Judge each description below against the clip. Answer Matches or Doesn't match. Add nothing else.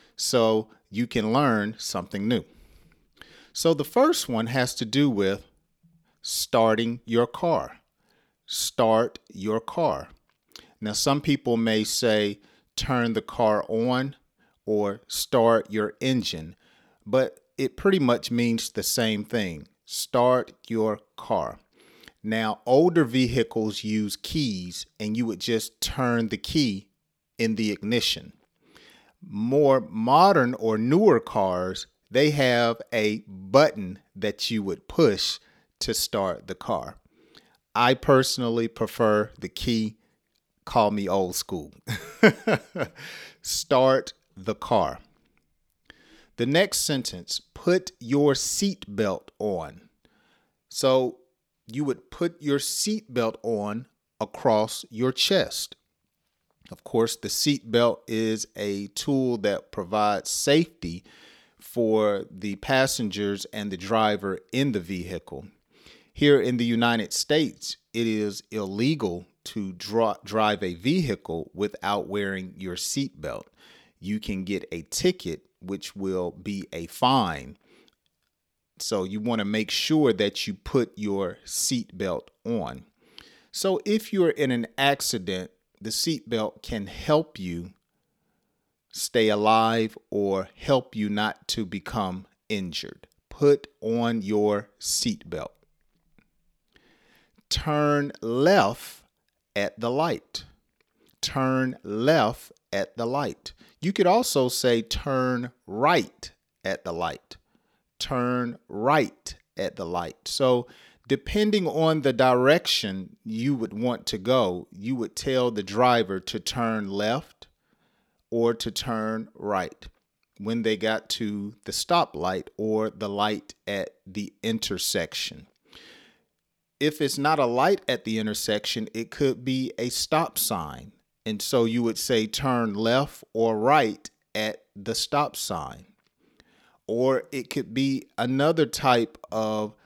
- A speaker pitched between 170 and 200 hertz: Doesn't match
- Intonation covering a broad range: Doesn't match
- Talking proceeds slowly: Matches